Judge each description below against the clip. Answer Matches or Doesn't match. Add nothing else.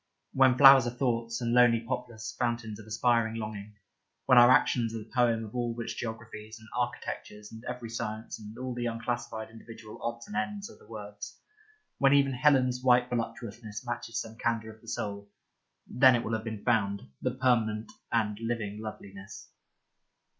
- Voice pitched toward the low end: Matches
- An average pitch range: Doesn't match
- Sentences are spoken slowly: Doesn't match